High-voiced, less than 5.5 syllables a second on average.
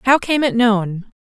Yes: high, 230 Hz; 4.1 syllables/s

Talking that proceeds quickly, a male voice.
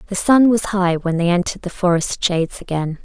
No: fast, 215 wpm; female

